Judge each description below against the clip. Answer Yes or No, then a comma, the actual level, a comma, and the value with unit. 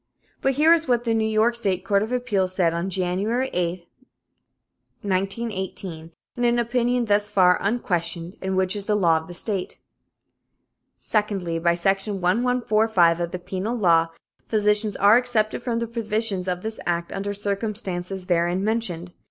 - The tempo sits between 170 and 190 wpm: No, average, 160 wpm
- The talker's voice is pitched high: Yes, high, 200 Hz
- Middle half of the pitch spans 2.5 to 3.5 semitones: No, average, 3.9 semitones